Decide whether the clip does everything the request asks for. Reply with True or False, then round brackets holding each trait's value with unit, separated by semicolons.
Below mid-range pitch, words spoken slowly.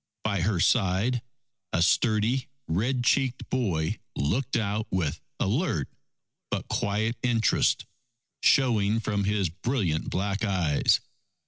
True (105 Hz; 110 wpm)